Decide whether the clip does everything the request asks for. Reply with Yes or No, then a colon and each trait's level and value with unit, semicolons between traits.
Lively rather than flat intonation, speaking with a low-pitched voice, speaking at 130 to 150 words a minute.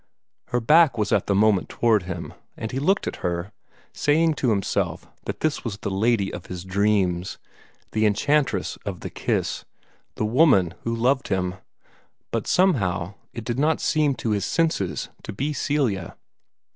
No: wide, 6.6 semitones; low, 110 Hz; average, 165 wpm